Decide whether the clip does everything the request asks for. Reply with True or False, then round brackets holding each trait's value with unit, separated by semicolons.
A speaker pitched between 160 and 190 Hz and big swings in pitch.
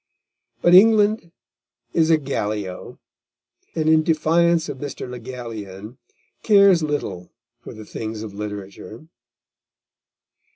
False (135 Hz; 7.7 semitones)